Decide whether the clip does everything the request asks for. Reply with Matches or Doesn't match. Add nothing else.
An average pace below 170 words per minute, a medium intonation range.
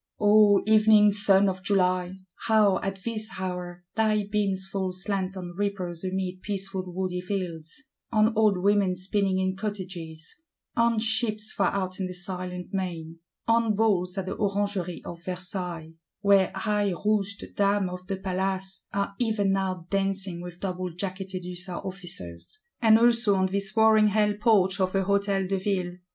Doesn't match